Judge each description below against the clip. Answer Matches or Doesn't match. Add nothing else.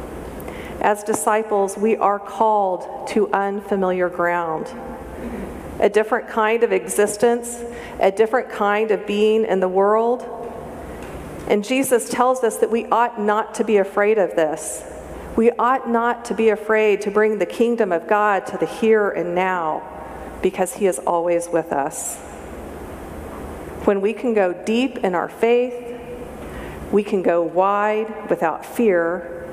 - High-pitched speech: Matches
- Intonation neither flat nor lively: Matches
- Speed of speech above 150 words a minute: Doesn't match